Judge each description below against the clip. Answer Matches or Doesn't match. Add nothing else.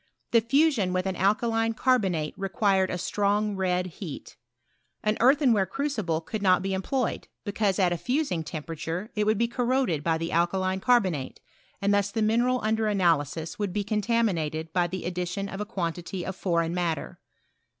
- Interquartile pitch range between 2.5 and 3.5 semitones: Doesn't match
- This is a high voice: Matches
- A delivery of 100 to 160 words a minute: Doesn't match